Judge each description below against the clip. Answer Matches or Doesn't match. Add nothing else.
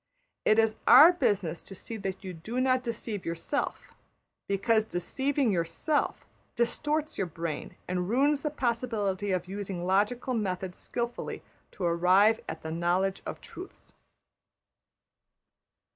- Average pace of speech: Doesn't match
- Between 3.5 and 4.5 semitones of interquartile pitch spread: Doesn't match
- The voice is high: Matches